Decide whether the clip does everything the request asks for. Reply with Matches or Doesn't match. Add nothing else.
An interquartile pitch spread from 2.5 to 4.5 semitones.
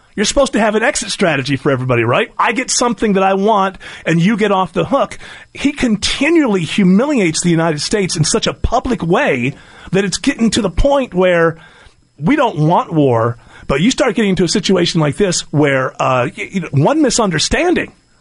Doesn't match